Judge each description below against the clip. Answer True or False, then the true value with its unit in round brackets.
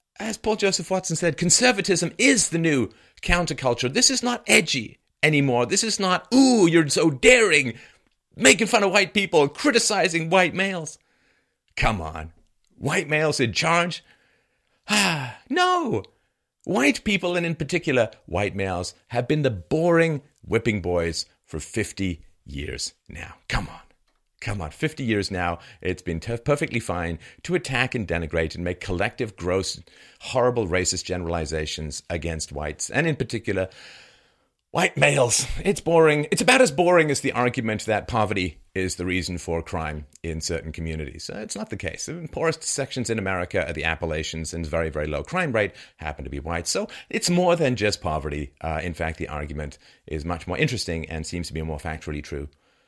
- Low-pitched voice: True (110 Hz)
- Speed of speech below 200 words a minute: True (170 wpm)